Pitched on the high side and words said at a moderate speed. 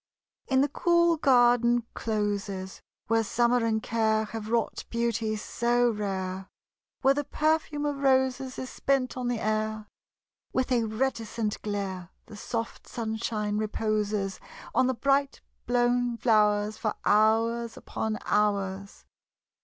No: high, 225 Hz; slow, 125 wpm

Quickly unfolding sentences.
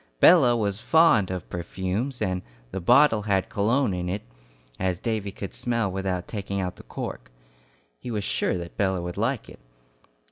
No: average, 170 wpm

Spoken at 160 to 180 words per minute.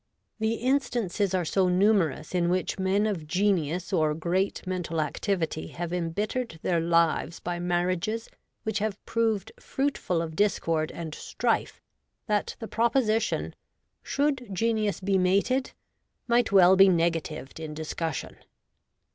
No: slow, 135 wpm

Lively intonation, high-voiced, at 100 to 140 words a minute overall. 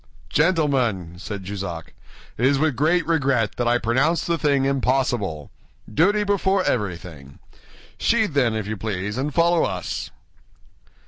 No: wide, 7.8 semitones; low, 130 Hz; slow, 135 wpm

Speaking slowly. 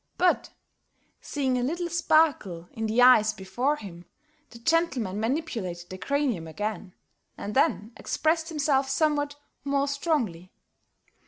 Yes: slow, 120 wpm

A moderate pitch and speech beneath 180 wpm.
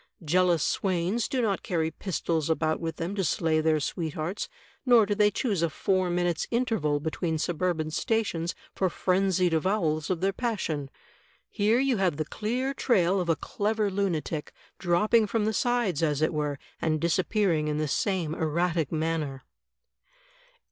Yes: medium, 175 Hz; average, 155 wpm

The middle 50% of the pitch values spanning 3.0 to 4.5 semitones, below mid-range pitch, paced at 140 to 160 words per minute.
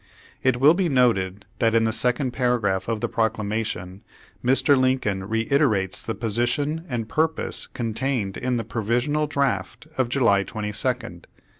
Yes: average, 3.7 semitones; low, 120 Hz; average, 150 wpm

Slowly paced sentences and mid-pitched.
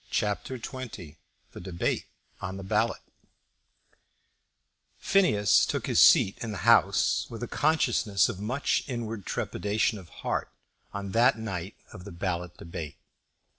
No: slow, 130 wpm; low, 105 Hz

